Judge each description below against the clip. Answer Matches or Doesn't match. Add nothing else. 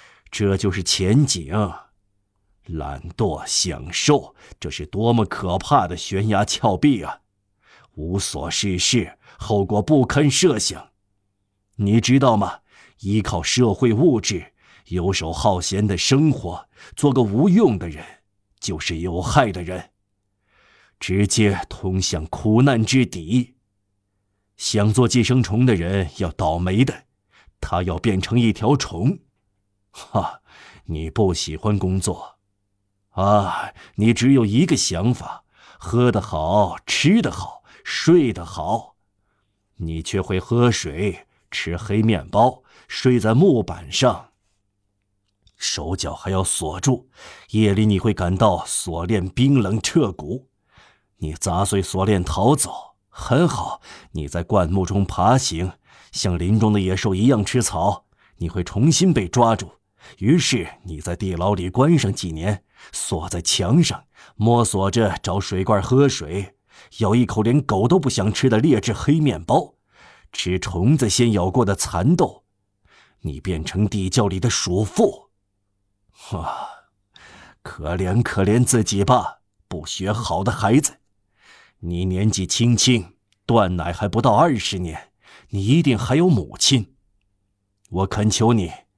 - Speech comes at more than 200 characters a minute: Doesn't match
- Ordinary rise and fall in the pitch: Matches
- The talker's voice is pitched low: Matches